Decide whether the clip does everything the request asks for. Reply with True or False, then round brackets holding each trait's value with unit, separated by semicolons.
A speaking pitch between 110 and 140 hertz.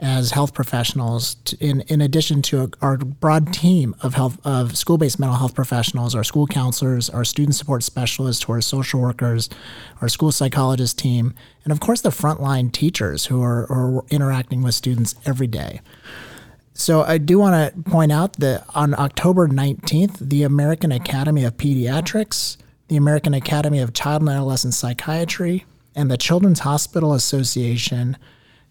True (135 Hz)